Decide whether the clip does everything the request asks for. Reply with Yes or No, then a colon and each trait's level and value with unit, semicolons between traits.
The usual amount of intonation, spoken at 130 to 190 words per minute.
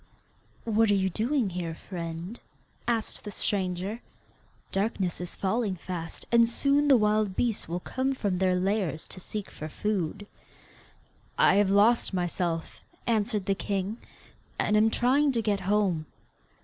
Yes: average, 3.6 semitones; average, 145 wpm